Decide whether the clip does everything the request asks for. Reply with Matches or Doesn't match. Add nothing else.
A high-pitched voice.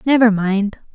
Matches